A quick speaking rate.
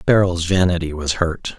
No: average, 150 wpm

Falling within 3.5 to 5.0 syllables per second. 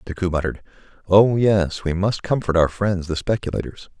No: 5.3 syllables/s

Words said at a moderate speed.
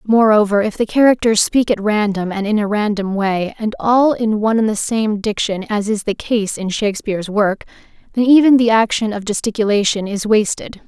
Yes: average, 195 wpm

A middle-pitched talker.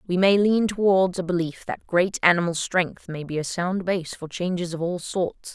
Yes: medium, 180 Hz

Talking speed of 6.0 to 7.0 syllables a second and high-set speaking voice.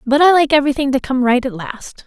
Yes: 6.2 syllables/s; very high, 270 Hz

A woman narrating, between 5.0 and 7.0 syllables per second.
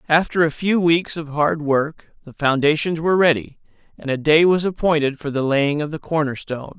No: male; 5.3 syllables/s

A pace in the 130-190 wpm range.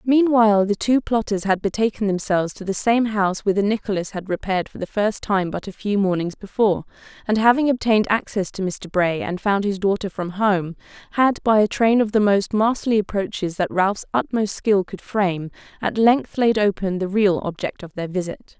No: average, 200 wpm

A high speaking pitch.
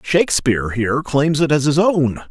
No: medium, 140 Hz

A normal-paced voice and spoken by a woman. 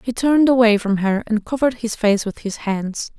No: fast, 225 wpm; female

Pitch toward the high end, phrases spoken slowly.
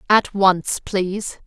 Yes: high, 195 Hz; slow, 125 wpm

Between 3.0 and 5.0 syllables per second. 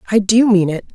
No: 6.1 syllables/s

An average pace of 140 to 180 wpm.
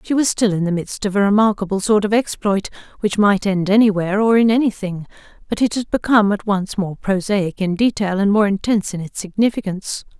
No: fast, 205 wpm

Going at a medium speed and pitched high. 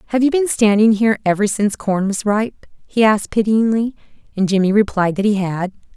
Yes: average, 190 wpm; high, 210 Hz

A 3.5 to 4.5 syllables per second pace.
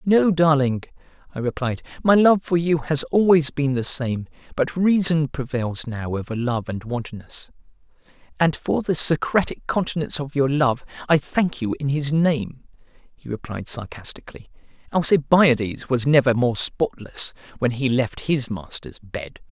Yes: 4.3 syllables/s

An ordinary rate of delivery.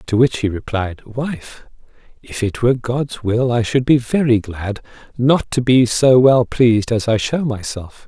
Yes: average, 185 wpm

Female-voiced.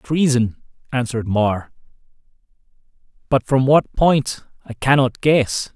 No: male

